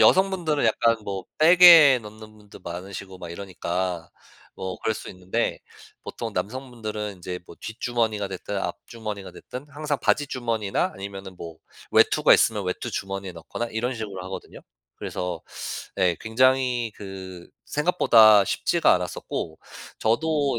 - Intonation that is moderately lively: Yes, average, 4.8 semitones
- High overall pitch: No, low, 105 Hz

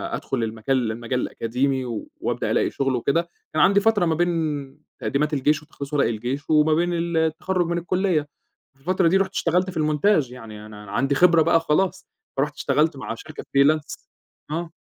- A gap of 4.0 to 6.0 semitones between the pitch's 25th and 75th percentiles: Yes, average, 4.4 semitones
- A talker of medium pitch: Yes, medium, 150 Hz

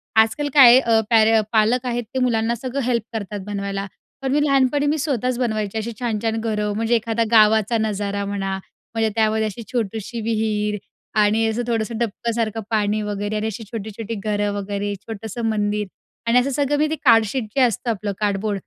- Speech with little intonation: Yes, narrow, 2.1 semitones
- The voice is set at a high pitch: Yes, high, 220 Hz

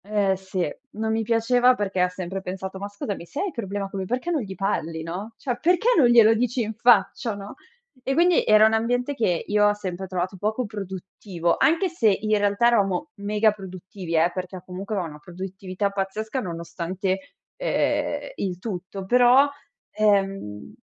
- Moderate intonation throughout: Yes, average, 3.4 semitones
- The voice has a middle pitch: No, high, 200 Hz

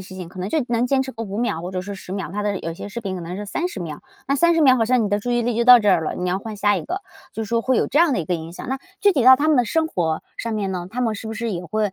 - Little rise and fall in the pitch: No, average, 5.0 semitones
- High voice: Yes, high, 215 Hz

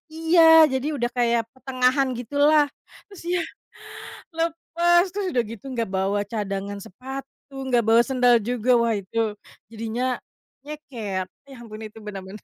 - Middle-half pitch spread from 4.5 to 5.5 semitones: Yes, average, 4.9 semitones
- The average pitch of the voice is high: Yes, high, 245 Hz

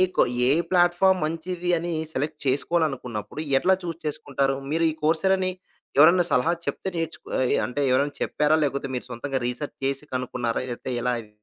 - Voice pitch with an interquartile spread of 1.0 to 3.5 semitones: No, average, 4.5 semitones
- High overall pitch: No, medium, 150 Hz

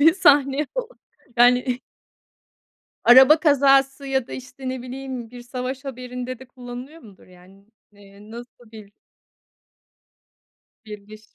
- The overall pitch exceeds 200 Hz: Yes, very high, 250 Hz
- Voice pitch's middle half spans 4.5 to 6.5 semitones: No, narrow, 2.6 semitones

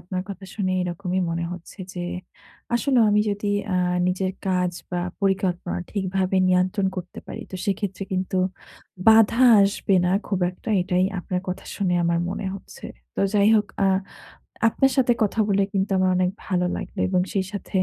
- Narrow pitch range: Yes, narrow, 1.8 semitones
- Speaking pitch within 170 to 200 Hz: Yes, high, 190 Hz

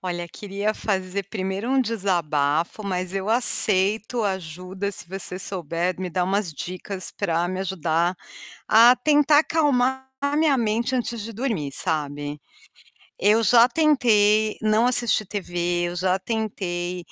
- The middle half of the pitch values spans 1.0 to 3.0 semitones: No, average, 4.5 semitones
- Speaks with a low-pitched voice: No, high, 195 Hz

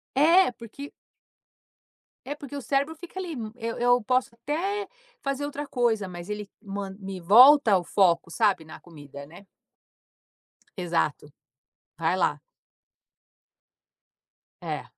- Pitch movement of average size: No, wide, 7.6 semitones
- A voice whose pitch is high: Yes, high, 225 Hz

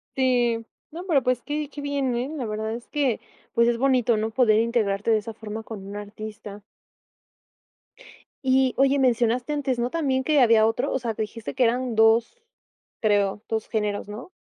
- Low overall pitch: No, high, 235 Hz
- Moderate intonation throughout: Yes, average, 3.2 semitones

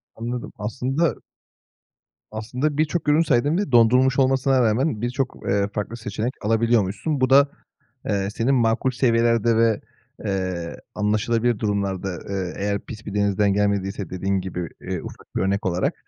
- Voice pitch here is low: Yes, low, 115 Hz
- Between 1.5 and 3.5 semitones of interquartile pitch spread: No, average, 4.2 semitones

